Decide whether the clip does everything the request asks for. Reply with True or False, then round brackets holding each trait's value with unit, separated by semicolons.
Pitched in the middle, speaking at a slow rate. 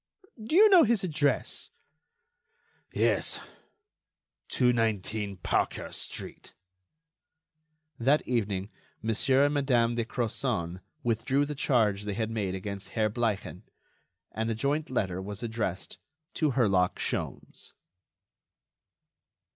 False (115 Hz; 105 wpm)